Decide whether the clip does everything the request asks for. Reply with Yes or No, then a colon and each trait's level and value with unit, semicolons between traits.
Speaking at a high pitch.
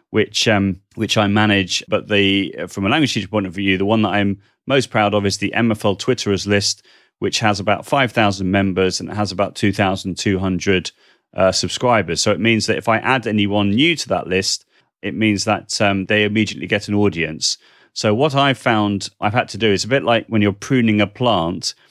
No: low, 105 Hz